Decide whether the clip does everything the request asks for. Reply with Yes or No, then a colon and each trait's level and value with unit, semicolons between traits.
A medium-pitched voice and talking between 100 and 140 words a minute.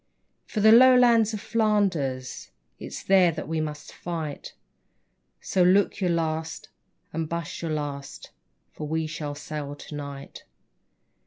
Yes: medium, 160 Hz; slow, 135 wpm